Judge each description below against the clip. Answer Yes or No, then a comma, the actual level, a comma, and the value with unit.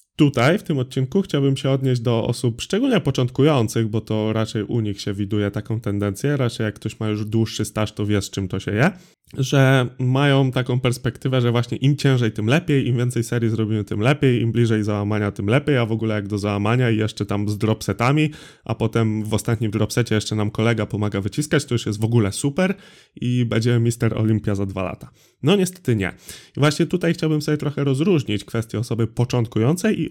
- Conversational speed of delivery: No, fast, 205 wpm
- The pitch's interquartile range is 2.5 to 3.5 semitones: No, average, 4.2 semitones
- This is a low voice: Yes, low, 115 Hz